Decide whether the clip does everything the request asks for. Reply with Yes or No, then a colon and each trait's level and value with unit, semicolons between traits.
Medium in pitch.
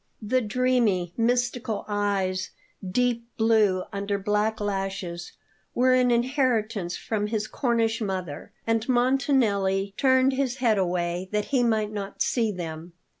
No: high, 215 Hz